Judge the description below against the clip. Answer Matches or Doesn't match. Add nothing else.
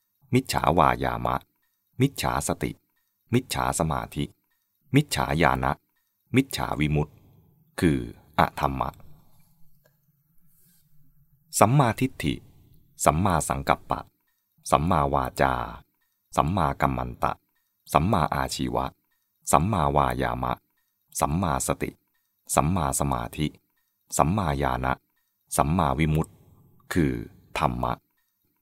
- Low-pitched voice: Matches